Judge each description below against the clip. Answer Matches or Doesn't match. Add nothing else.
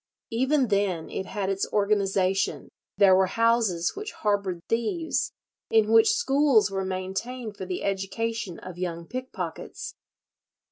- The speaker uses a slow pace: Matches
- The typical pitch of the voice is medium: Doesn't match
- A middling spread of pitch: Matches